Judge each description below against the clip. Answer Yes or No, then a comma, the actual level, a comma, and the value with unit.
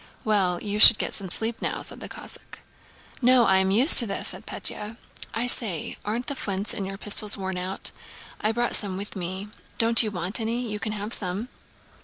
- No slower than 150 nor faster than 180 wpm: No, fast, 205 wpm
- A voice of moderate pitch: No, high, 210 Hz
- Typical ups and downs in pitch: Yes, average, 3.0 semitones